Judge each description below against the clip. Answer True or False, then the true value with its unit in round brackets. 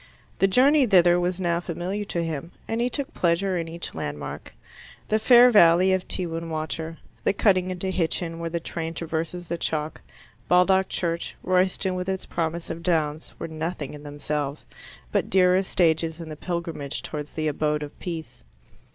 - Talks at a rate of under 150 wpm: False (175 wpm)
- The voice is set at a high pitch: False (170 Hz)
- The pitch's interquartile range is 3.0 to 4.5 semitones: False (2.6 semitones)